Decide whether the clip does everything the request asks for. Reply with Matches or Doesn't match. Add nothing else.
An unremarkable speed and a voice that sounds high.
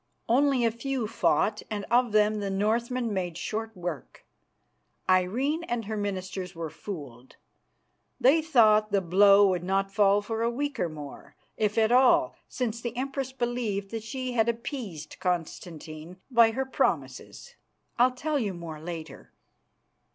Matches